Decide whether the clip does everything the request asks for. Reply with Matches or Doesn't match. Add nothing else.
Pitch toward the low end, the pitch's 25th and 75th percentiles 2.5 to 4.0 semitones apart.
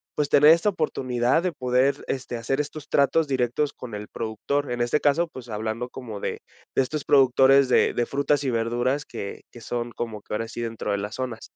Matches